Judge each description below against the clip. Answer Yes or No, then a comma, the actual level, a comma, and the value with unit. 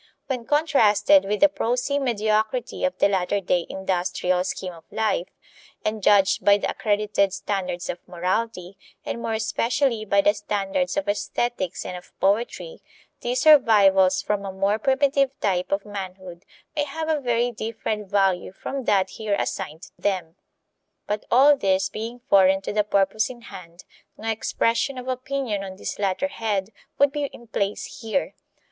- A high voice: Yes, high, 210 Hz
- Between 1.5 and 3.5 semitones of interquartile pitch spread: No, average, 4.2 semitones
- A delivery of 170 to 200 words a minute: No, average, 160 wpm